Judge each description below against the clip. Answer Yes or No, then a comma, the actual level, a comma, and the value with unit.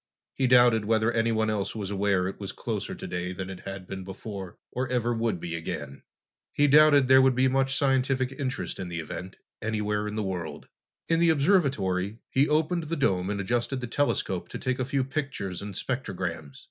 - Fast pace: No, average, 195 wpm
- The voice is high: No, low, 110 Hz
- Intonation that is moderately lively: No, wide, 5.7 semitones